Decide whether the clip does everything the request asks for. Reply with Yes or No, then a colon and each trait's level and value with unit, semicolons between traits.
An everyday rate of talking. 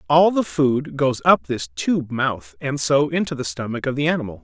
No: fast, 215 wpm